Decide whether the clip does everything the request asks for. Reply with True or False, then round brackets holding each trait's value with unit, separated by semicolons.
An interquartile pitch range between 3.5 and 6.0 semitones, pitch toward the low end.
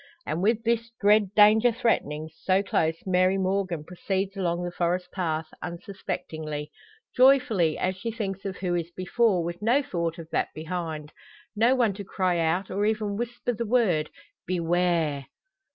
False (3.8 semitones; 185 Hz)